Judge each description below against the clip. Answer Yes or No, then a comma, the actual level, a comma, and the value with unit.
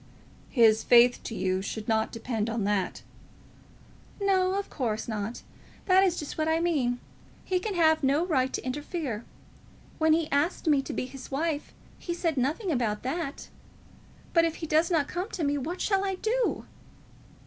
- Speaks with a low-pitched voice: No, very high, 295 Hz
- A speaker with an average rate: Yes, average, 175 wpm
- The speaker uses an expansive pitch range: Yes, wide, 6.1 semitones